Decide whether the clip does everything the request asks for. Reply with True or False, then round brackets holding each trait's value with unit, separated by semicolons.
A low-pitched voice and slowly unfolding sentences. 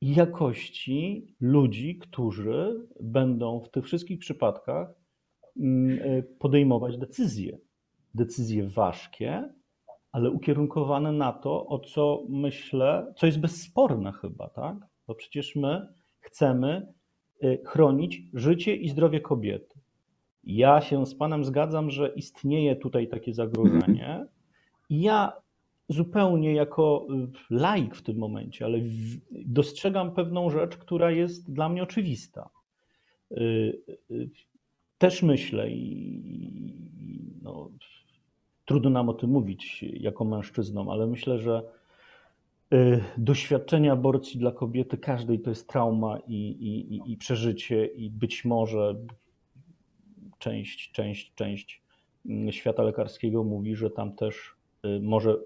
True (130 Hz; 105 wpm)